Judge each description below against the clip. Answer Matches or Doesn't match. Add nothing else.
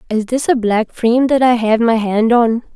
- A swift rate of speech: Matches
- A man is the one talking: Doesn't match